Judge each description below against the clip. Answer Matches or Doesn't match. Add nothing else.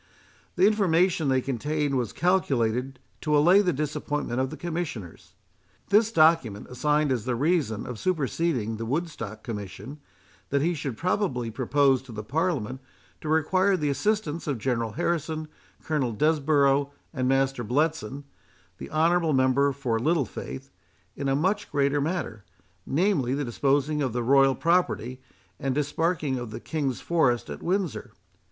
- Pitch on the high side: Doesn't match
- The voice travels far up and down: Doesn't match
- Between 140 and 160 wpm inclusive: Matches